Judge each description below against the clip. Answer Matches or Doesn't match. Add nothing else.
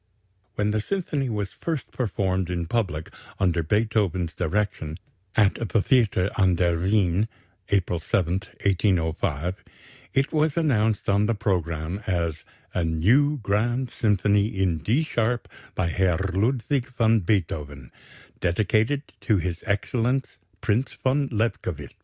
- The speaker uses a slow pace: Matches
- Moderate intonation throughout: Matches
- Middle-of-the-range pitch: Doesn't match